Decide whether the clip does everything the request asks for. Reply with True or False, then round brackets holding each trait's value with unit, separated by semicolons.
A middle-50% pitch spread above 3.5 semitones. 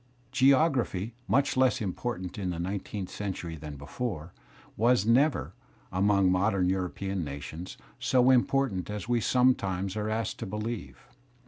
True (5.1 semitones)